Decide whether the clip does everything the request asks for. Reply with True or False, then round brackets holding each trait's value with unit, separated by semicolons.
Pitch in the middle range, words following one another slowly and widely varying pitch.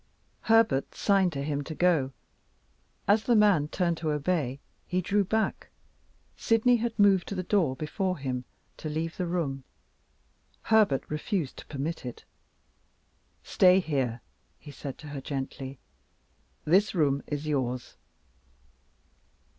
True (160 Hz; 130 wpm; 5.7 semitones)